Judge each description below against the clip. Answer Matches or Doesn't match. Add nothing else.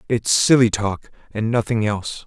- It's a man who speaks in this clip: Matches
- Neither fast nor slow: Matches